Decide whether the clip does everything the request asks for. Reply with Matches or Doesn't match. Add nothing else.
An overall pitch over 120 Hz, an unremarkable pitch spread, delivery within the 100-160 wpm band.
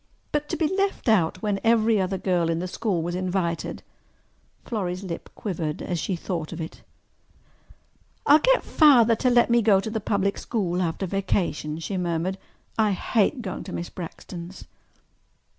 Doesn't match